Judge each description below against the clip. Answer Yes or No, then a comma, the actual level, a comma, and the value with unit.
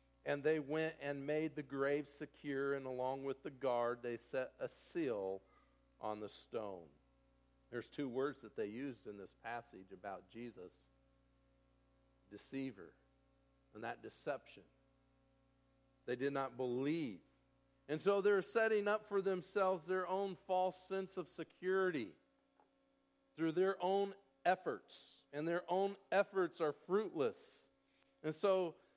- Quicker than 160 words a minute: No, slow, 135 wpm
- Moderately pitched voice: Yes, medium, 150 Hz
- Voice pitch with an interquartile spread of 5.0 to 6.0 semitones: Yes, wide, 5.6 semitones